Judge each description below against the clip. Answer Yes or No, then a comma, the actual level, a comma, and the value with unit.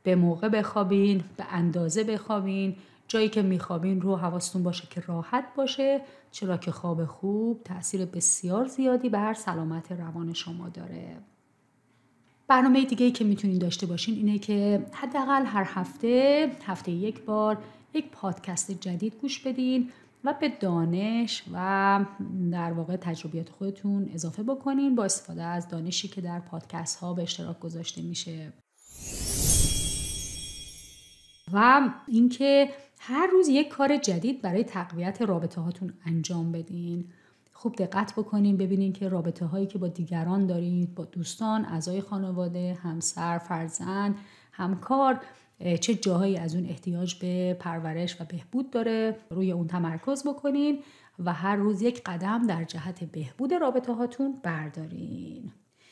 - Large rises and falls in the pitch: No, average, 4.5 semitones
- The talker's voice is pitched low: No, high, 190 Hz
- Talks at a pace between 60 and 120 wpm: No, average, 135 wpm